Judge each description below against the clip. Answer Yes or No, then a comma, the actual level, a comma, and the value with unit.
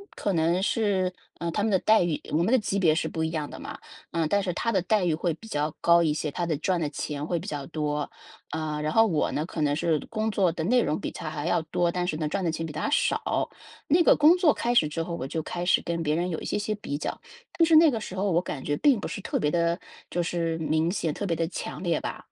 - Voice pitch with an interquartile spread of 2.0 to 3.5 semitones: No, average, 4.3 semitones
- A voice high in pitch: No, medium, 170 Hz